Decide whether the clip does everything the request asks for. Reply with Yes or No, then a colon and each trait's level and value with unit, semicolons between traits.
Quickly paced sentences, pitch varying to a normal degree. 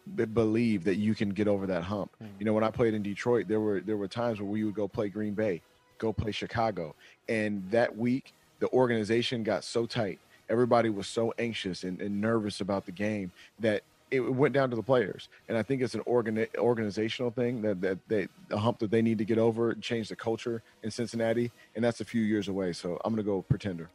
No: fast, 230 wpm; narrow, 2.1 semitones